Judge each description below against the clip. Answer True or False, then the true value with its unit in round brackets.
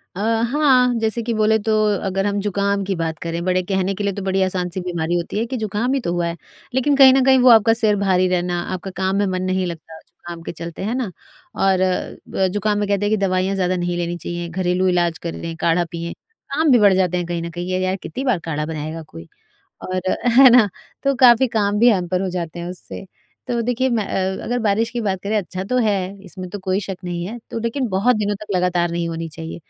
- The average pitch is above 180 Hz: True (190 Hz)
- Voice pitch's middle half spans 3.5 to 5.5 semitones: True (3.8 semitones)